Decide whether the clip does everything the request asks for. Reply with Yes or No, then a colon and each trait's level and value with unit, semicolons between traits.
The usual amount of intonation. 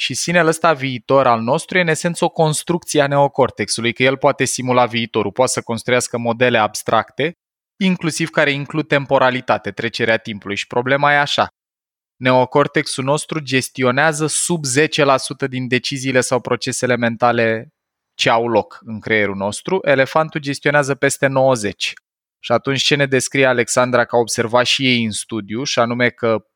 Yes: average, 3.5 semitones